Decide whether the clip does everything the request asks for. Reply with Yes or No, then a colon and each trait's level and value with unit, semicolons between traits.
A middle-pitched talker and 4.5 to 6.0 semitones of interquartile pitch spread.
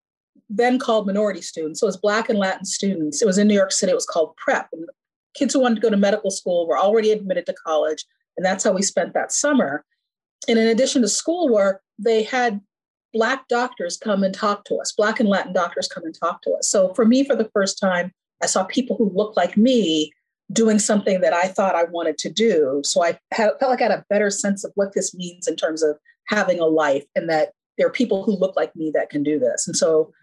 No: high, 205 Hz; average, 4.8 semitones